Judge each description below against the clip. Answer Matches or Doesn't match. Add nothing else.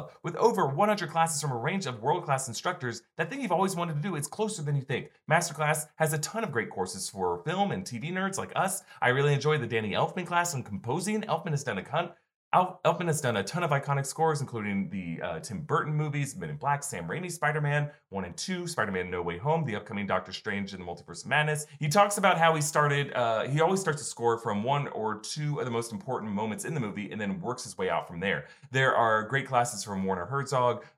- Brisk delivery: Matches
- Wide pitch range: Matches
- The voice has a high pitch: Doesn't match